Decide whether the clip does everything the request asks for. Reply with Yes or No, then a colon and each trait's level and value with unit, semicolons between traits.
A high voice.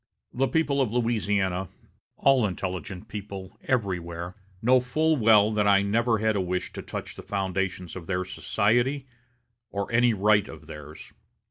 No: low, 105 Hz